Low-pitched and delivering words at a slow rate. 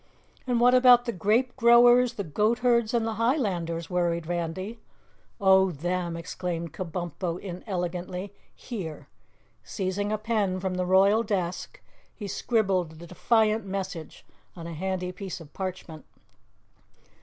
No: high, 190 Hz; slow, 125 wpm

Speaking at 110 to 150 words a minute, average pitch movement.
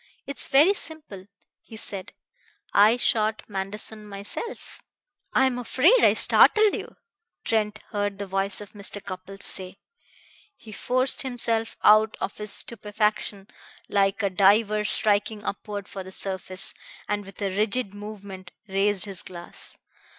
No: slow, 135 wpm; narrow, 2.1 semitones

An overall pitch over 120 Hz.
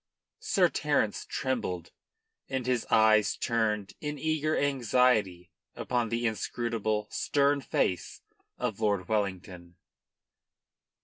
No: low, 110 Hz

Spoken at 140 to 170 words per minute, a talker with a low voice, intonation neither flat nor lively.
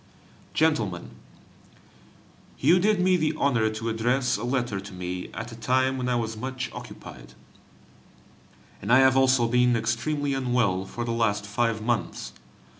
Yes: average, 150 wpm; low, 120 Hz; average, 3.2 semitones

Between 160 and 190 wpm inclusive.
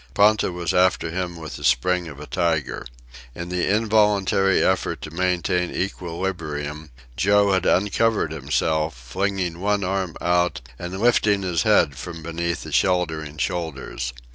No: average, 140 wpm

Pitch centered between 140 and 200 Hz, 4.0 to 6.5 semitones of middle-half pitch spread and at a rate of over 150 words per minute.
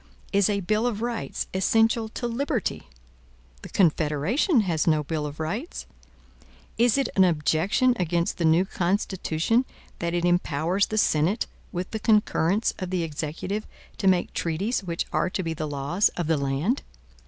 Yes: medium, 185 Hz; average, 5.2 semitones; average, 160 wpm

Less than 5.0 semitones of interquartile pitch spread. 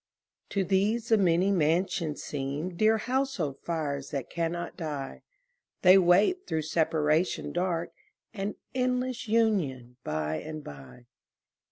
No: wide, 5.6 semitones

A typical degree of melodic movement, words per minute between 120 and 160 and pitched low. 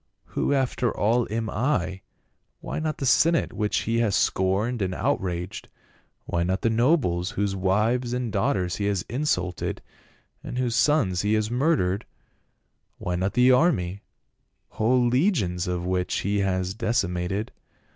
Yes: average, 5.0 semitones; average, 155 wpm; low, 105 Hz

